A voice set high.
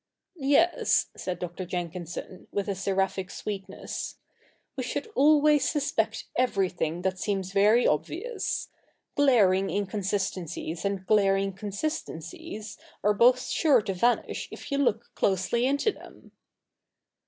Yes: high, 200 Hz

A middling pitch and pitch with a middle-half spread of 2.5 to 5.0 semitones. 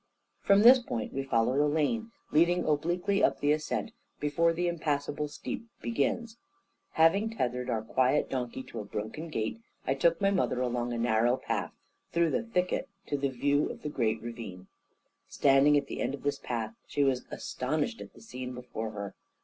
No: medium, 145 Hz; wide, 5.5 semitones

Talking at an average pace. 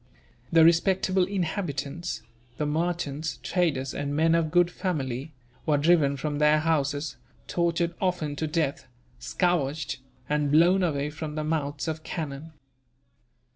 No: slow, 130 wpm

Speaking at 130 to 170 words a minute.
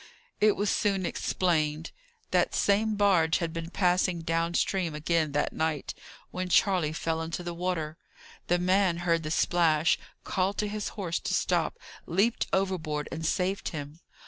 Yes: average, 155 wpm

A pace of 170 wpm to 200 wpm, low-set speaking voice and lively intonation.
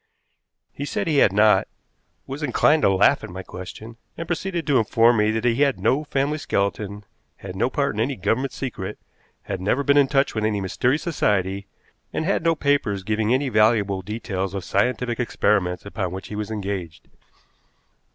Yes: average, 180 wpm; low, 110 Hz; wide, 5.7 semitones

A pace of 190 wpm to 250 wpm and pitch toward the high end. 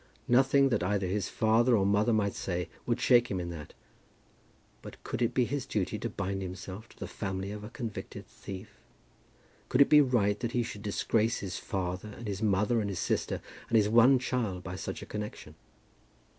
No: average, 200 wpm; low, 105 Hz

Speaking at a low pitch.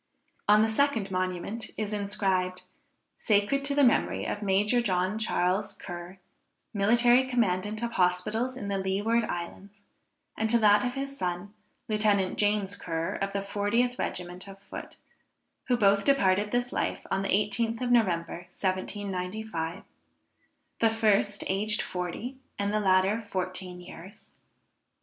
No: high, 205 Hz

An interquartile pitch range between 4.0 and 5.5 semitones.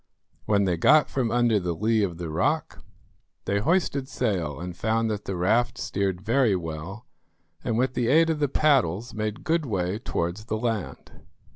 Yes: average, 5.2 semitones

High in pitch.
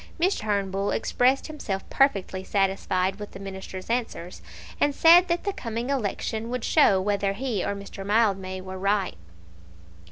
Yes: high, 205 Hz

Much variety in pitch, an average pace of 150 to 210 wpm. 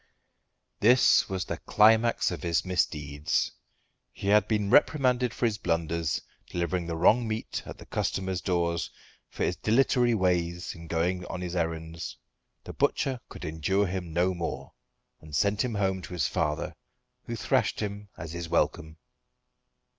No: average, 4.0 semitones; average, 155 wpm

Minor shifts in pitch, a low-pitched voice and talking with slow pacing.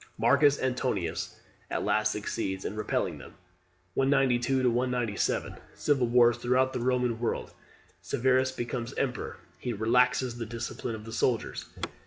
Yes: narrow, 2.2 semitones; low, 120 Hz; slow, 130 wpm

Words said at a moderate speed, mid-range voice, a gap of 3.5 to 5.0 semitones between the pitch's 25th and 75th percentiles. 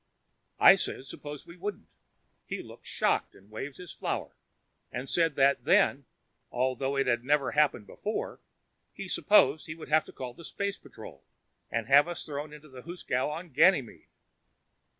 Yes: average, 165 wpm; medium, 145 Hz; average, 4.1 semitones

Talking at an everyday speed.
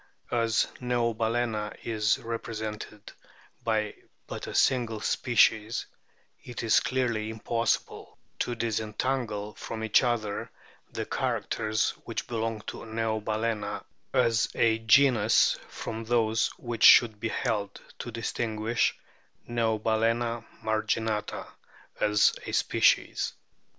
No: slow, 105 wpm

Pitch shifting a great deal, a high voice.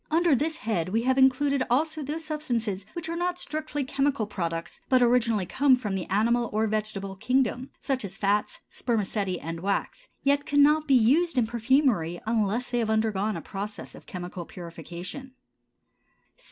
Yes: wide, 5.8 semitones; high, 235 Hz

